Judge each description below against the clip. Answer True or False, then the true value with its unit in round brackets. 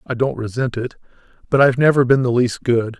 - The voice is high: False (125 Hz)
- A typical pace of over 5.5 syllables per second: True (6.0 syllables/s)